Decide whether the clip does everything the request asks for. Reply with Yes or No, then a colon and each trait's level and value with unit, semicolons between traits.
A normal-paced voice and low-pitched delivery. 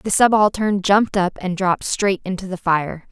No: average, 195 wpm; high, 190 Hz